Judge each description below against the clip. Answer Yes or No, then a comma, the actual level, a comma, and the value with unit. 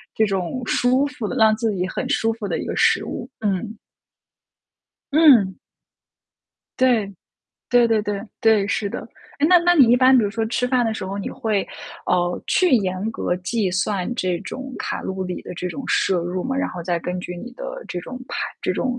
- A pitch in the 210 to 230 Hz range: Yes, high, 220 Hz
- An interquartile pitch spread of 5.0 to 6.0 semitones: Yes, average, 5.3 semitones